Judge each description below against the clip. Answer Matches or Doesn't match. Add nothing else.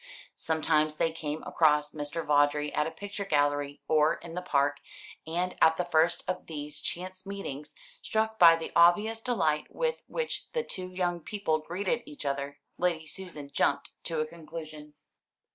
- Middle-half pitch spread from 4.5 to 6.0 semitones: Doesn't match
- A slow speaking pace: Doesn't match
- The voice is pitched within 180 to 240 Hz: Doesn't match